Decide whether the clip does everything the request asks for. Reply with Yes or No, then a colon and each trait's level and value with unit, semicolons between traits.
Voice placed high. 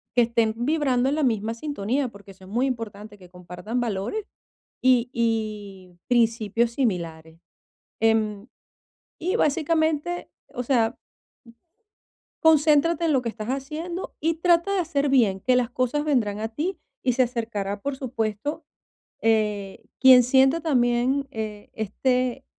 Yes: high, 240 Hz